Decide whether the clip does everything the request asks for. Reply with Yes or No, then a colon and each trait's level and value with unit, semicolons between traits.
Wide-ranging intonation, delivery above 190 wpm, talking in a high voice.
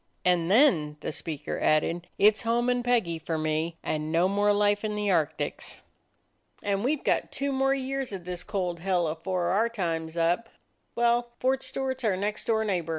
Yes: wide, 6.0 semitones; average, 200 wpm; high, 195 Hz